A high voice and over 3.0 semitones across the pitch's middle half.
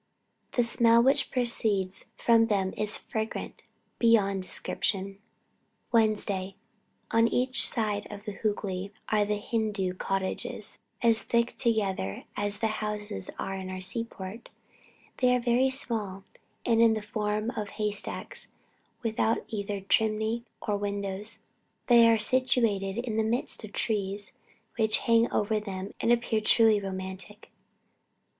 No: high, 215 Hz; narrow, 2.5 semitones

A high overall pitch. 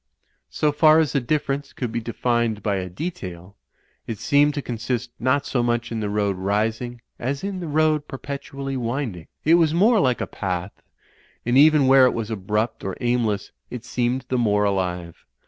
No: low, 120 Hz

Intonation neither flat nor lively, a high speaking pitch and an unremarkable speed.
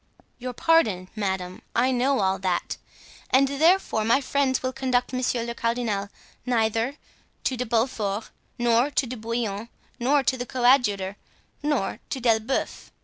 Yes: average, 3.2 semitones; high, 240 Hz; average, 145 wpm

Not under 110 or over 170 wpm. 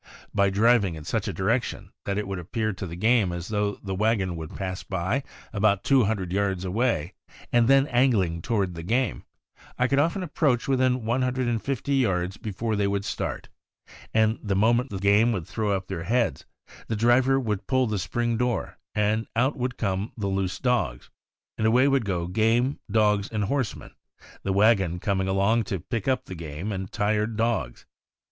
No: average, 185 wpm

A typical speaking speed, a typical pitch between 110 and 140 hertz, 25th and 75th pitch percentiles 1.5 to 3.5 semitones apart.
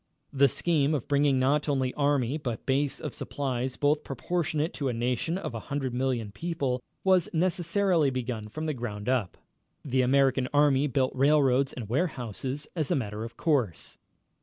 Yes: average, 165 wpm; low, 135 Hz; average, 3.0 semitones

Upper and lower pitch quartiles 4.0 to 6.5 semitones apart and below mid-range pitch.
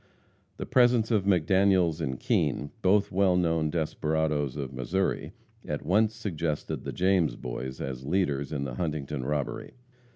Yes: average, 5.1 semitones; very low, 80 Hz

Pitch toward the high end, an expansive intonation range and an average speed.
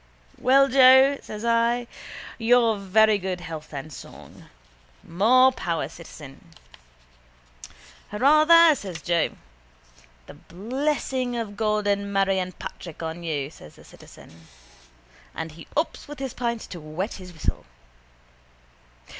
No: high, 205 Hz; wide, 6.8 semitones; slow, 125 wpm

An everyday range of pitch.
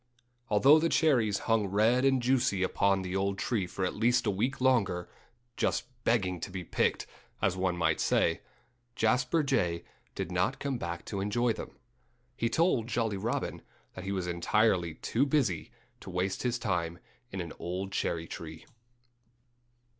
Yes: average, 5.0 semitones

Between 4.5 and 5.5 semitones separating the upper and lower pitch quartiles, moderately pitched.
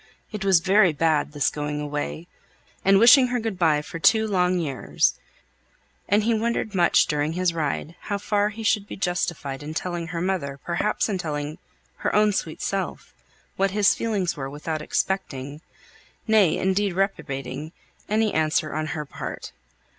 Yes: average, 5.1 semitones; medium, 175 Hz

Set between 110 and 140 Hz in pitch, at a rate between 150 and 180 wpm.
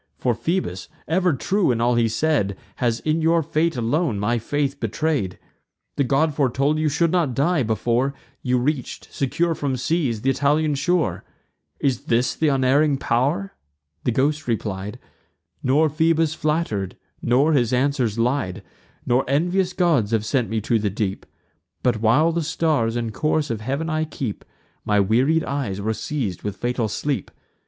Yes: low, 135 Hz; average, 160 wpm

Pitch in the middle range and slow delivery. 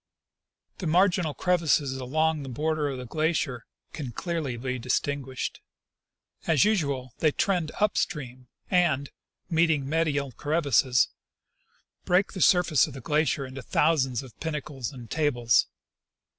Yes: medium, 150 Hz; slow, 130 wpm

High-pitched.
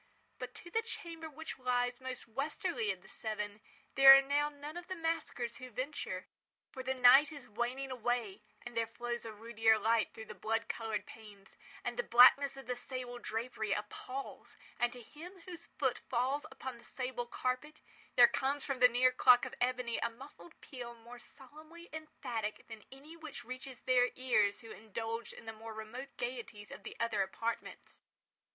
Yes: very high, 250 Hz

